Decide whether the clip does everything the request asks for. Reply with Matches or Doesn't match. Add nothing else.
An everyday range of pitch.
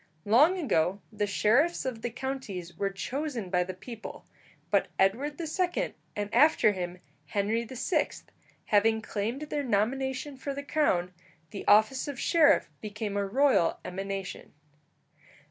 Doesn't match